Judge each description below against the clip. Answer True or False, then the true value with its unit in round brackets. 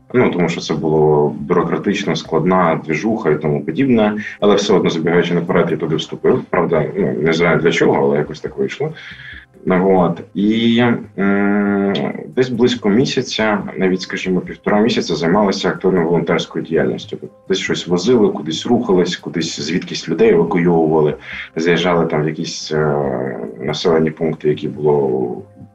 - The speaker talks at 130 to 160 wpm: True (150 wpm)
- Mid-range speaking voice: False (85 Hz)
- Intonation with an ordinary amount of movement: True (4.4 semitones)